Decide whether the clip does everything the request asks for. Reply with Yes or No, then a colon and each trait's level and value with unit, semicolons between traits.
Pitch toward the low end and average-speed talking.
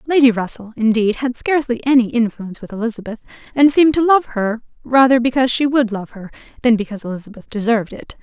No: high, 240 Hz; average, 180 wpm